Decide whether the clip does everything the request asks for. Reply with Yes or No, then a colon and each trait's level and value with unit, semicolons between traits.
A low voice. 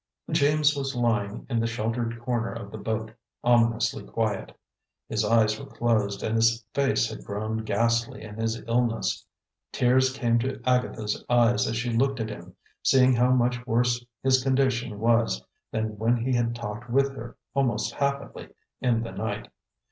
Yes: low, 115 Hz